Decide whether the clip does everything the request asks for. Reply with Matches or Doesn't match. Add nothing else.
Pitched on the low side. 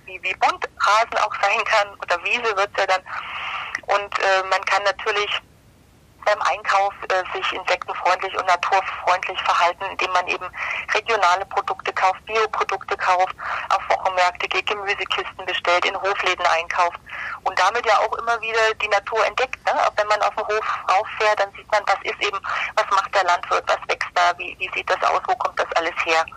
Doesn't match